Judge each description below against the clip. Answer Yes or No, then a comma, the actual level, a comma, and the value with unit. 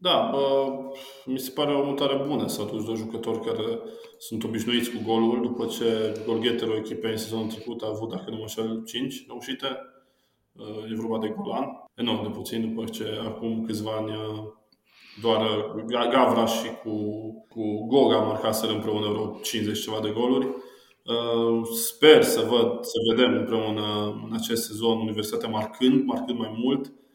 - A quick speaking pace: No, average, 155 wpm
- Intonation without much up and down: Yes, narrow, 1.8 semitones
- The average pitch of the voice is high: No, low, 115 Hz